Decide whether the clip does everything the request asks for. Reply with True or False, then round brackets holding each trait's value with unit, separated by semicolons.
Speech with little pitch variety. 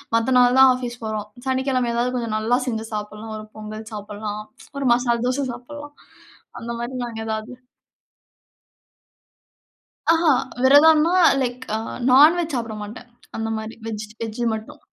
False (3.2 semitones)